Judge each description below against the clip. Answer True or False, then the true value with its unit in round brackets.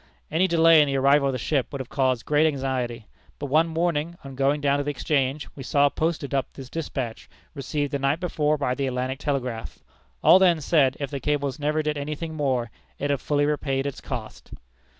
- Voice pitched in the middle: True (145 Hz)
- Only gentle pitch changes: True (2.2 semitones)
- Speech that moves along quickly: True (210 wpm)